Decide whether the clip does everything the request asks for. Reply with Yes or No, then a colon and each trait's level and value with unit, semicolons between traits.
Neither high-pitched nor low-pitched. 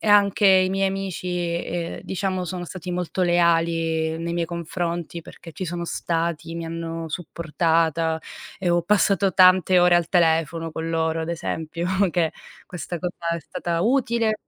Yes: medium, 170 Hz